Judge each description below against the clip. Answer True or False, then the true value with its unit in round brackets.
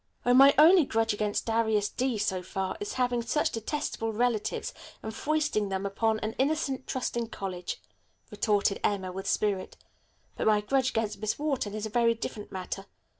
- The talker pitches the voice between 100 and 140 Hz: False (220 Hz)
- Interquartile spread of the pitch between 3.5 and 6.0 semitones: True (3.9 semitones)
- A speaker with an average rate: True (175 wpm)